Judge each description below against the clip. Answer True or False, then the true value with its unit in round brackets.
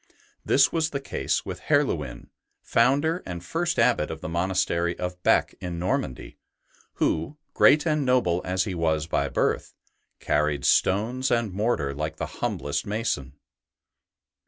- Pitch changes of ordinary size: False (8.3 semitones)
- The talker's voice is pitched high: False (90 Hz)